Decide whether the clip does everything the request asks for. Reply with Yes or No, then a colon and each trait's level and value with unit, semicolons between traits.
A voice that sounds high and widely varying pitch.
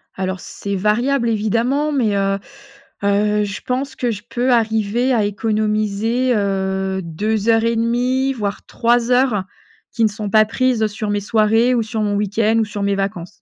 No: high, 215 Hz; average, 2.7 semitones